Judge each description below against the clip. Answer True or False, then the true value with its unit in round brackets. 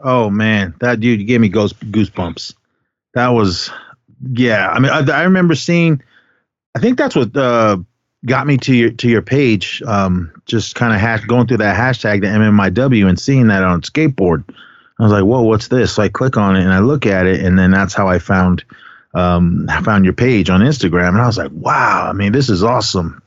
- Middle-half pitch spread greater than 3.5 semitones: True (4.6 semitones)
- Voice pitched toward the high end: False (110 Hz)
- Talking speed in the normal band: False (210 wpm)